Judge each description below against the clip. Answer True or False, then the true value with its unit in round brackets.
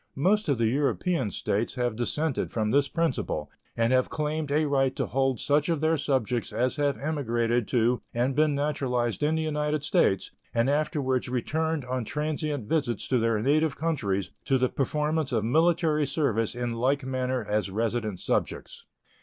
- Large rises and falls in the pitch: False (4.2 semitones)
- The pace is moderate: True (170 wpm)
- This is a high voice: False (135 Hz)